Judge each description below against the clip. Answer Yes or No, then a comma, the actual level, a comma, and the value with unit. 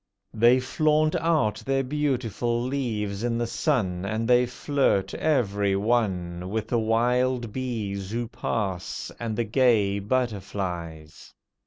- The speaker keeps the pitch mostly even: No, average, 4.2 semitones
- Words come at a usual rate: No, slow, 125 wpm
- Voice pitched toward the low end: Yes, low, 115 Hz